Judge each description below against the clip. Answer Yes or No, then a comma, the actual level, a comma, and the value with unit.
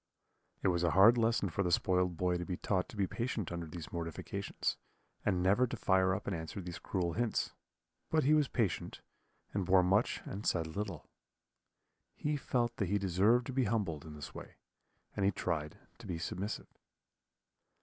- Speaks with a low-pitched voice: Yes, very low, 95 Hz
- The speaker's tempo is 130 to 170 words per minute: No, average, 185 wpm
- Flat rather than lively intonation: No, average, 4.0 semitones